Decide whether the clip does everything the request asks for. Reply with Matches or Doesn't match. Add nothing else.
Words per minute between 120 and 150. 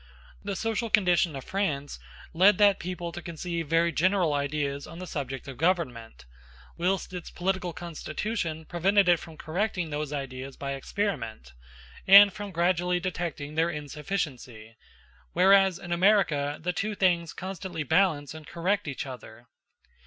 Matches